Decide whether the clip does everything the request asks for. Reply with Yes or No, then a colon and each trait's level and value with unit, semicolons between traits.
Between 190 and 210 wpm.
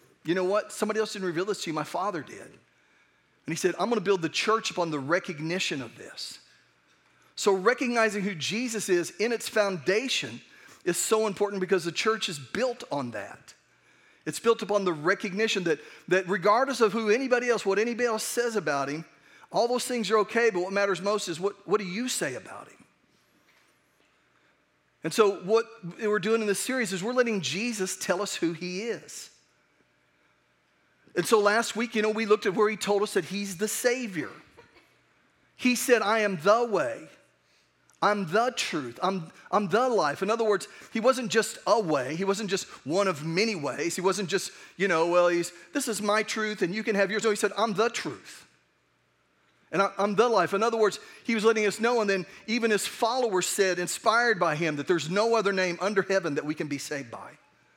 Yes: fast, 205 wpm